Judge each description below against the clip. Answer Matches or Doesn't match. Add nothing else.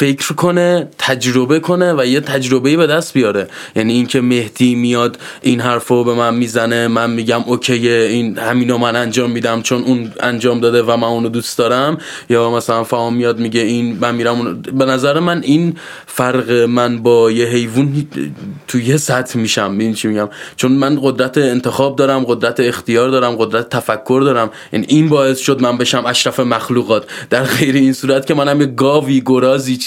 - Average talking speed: Doesn't match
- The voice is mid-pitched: Doesn't match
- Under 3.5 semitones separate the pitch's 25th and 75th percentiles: Matches